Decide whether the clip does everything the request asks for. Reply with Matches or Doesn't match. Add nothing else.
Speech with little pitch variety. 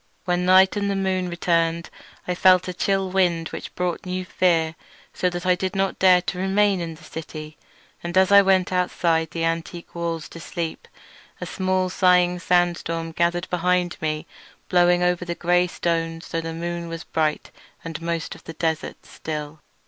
Matches